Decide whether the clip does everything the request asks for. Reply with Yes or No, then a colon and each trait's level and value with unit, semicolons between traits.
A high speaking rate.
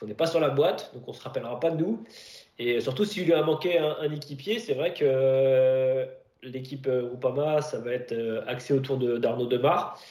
Yes: fast, 240 wpm